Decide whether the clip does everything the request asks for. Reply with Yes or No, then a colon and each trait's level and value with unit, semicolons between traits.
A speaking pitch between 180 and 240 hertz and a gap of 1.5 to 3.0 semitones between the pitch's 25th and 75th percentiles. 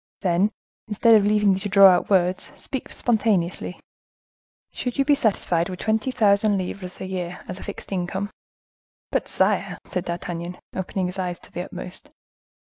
Yes: high, 190 Hz; narrow, 2.6 semitones